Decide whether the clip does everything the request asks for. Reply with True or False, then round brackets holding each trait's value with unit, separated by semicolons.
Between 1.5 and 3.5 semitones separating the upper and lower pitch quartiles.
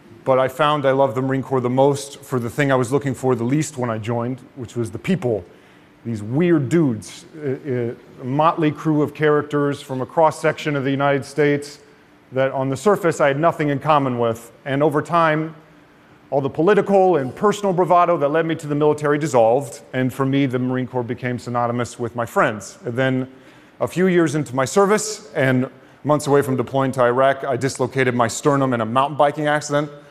True (2.9 semitones)